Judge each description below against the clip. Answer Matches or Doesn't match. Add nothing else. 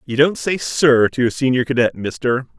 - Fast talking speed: Matches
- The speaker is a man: Matches